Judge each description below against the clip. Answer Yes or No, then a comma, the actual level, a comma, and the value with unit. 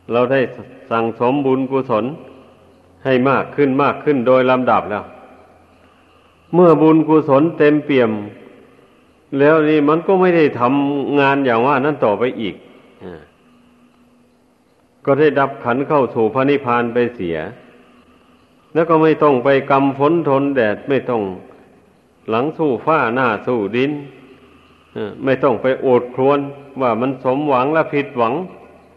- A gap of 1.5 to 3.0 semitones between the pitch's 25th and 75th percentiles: Yes, narrow, 2.4 semitones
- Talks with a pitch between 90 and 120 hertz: No, low, 135 Hz